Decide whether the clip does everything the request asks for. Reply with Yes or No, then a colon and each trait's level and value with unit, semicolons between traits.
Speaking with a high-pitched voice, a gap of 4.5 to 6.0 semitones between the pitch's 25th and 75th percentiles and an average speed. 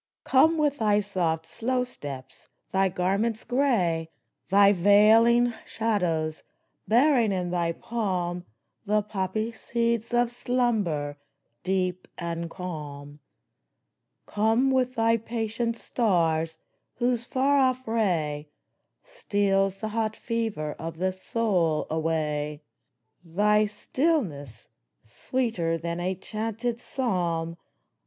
No: high, 205 Hz; wide, 5.6 semitones; slow, 105 wpm